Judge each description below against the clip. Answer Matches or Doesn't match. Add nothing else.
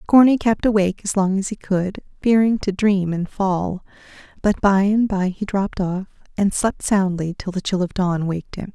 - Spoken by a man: Doesn't match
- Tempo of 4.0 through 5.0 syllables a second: Matches